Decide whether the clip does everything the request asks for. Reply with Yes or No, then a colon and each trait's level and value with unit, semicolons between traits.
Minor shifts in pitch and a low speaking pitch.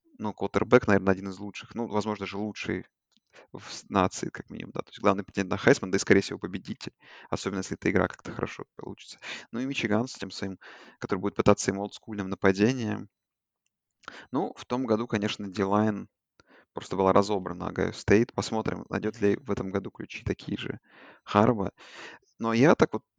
Yes: narrow, 2.3 semitones; low, 105 Hz